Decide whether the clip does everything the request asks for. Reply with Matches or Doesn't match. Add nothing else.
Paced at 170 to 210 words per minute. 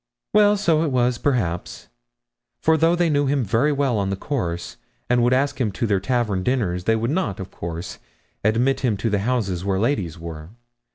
Matches